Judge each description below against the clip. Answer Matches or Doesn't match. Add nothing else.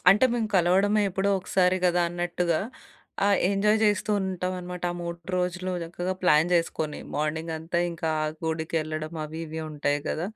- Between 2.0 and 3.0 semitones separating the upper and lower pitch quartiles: Matches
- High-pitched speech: Doesn't match